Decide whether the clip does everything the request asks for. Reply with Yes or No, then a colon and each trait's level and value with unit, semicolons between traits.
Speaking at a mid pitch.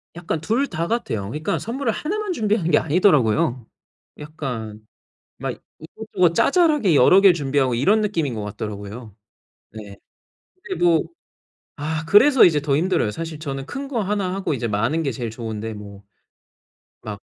Yes: medium, 155 Hz